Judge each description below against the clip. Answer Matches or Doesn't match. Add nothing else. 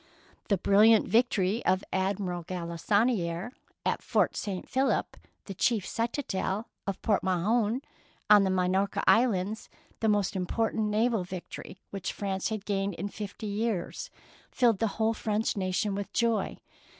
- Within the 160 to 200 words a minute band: Doesn't match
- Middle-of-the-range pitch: Doesn't match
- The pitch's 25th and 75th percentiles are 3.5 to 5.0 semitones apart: Doesn't match